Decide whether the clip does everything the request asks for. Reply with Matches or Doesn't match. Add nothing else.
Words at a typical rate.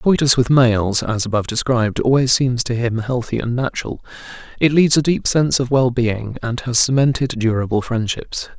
Matches